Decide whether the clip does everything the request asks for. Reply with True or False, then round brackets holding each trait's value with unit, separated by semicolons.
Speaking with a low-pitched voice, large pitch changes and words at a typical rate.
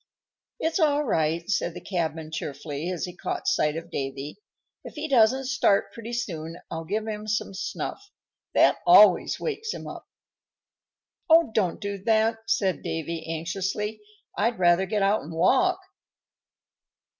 False (200 Hz; 6.0 semitones; 145 wpm)